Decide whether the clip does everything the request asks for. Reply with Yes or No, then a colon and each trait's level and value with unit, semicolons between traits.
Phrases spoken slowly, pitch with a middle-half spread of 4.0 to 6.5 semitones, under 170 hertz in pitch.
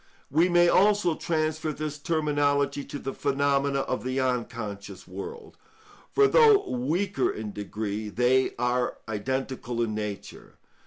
Yes: slow, 125 wpm; average, 4.8 semitones; medium, 140 Hz